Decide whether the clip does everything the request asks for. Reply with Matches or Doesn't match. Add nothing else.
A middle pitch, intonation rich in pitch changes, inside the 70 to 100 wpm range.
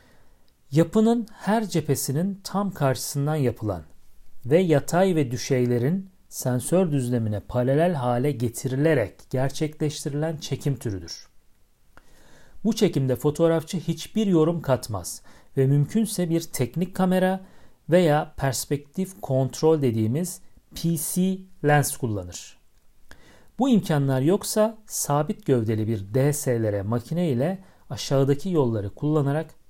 Matches